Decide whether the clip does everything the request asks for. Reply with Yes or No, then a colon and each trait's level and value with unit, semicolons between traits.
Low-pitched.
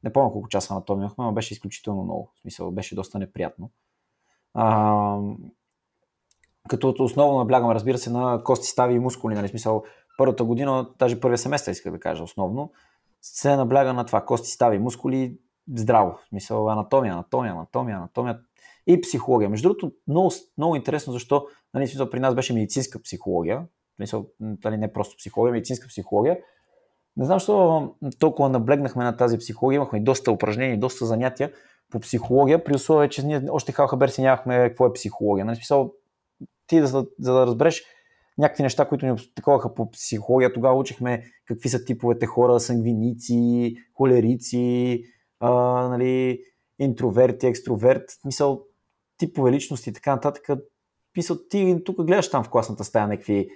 Yes: low, 125 Hz